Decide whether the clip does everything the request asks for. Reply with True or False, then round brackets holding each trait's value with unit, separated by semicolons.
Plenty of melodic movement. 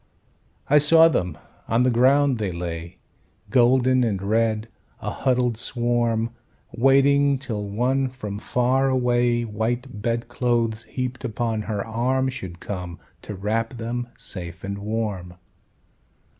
False (3.4 semitones)